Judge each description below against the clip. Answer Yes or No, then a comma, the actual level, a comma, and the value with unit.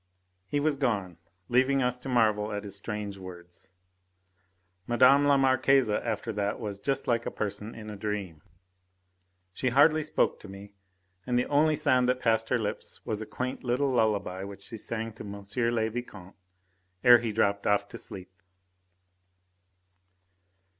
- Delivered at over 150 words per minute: Yes, average, 160 wpm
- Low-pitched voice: Yes, low, 110 Hz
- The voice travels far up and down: No, average, 3.9 semitones